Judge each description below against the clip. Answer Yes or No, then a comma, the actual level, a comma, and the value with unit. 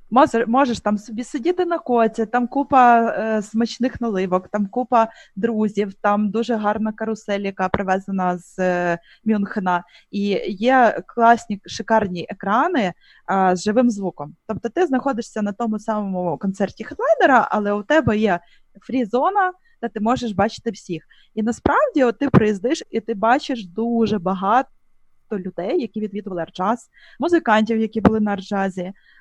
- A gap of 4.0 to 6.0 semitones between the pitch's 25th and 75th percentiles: No, average, 3.2 semitones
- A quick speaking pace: No, average, 145 wpm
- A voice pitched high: Yes, high, 220 Hz